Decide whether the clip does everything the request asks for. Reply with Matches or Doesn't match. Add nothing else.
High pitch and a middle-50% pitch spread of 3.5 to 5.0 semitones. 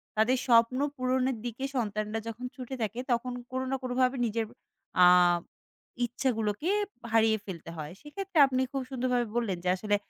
Doesn't match